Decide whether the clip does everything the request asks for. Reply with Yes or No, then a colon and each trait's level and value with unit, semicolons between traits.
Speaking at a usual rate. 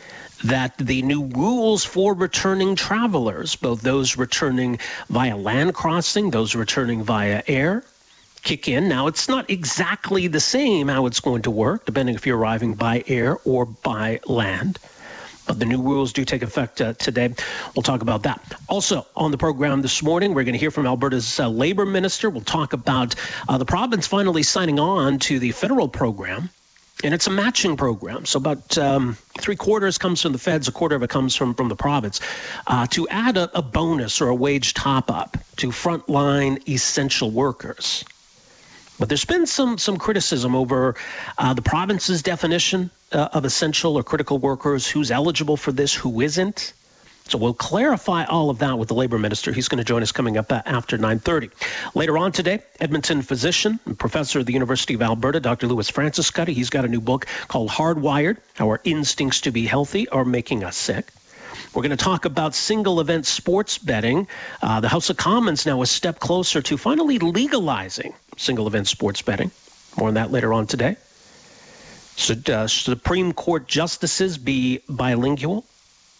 Yes: average, 180 wpm